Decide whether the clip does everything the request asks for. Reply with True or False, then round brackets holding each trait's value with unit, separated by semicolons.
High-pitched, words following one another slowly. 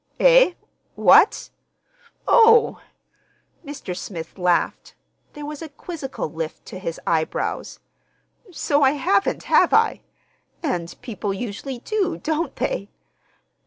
True (275 Hz; 110 wpm)